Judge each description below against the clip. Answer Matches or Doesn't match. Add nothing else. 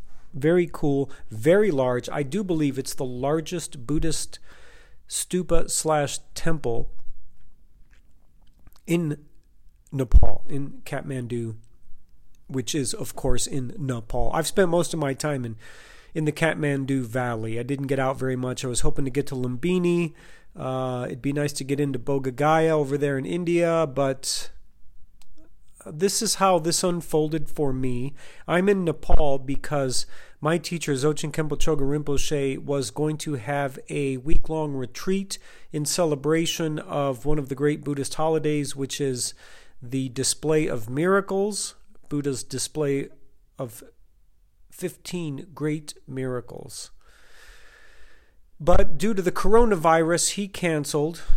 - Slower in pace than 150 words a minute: Matches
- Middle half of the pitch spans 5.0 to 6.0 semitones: Doesn't match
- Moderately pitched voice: Matches